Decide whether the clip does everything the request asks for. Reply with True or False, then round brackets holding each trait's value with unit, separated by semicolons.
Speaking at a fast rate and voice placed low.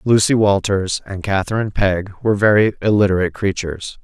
False (135 wpm; 100 Hz)